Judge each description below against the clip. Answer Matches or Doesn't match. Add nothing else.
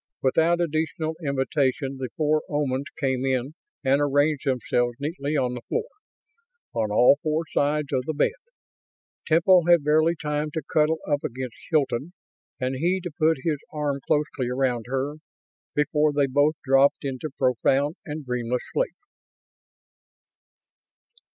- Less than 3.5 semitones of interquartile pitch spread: Matches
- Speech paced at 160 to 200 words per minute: Doesn't match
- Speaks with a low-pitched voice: Doesn't match